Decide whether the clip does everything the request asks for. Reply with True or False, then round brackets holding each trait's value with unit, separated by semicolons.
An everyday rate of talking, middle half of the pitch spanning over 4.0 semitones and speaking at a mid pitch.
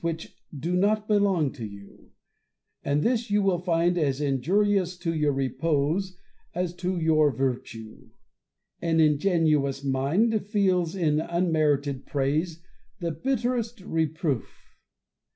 False (125 wpm; 4.6 semitones; 165 Hz)